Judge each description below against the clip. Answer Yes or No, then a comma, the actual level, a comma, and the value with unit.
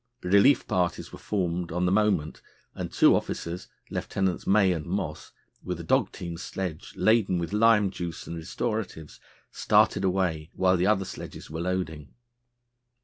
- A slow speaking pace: No, average, 150 wpm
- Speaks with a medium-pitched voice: No, very low, 90 Hz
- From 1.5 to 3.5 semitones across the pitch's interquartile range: Yes, average, 2.8 semitones